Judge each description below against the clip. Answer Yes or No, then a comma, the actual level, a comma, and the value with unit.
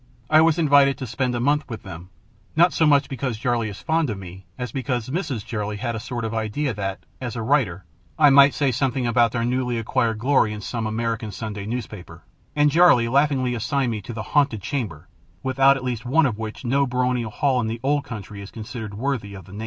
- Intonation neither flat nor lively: Yes, average, 4.1 semitones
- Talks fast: Yes, fast, 225 wpm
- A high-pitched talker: No, low, 120 Hz